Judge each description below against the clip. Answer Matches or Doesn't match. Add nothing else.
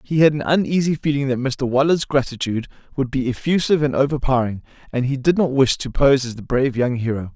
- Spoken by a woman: Doesn't match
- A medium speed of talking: Doesn't match